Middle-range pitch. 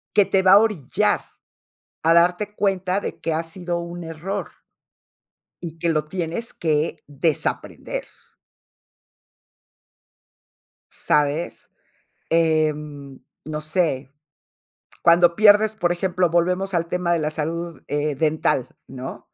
Yes: medium, 170 Hz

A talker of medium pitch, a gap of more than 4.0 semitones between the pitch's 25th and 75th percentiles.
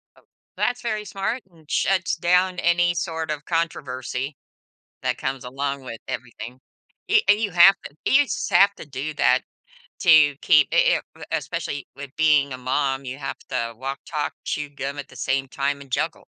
Yes: medium, 145 Hz; average, 4.4 semitones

